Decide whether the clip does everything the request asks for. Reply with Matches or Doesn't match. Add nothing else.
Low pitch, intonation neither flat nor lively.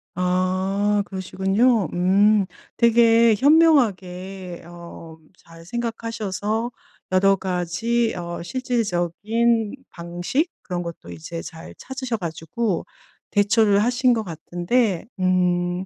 Doesn't match